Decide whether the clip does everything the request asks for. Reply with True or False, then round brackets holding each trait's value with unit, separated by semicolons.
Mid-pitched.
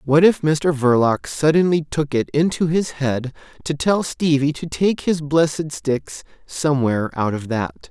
True (150 Hz)